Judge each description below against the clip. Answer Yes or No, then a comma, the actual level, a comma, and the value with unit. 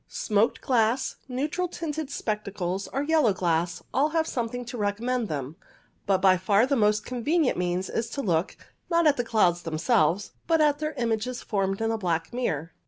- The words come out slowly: No, average, 175 wpm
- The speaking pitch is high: Yes, high, 225 Hz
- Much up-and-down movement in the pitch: Yes, wide, 6.2 semitones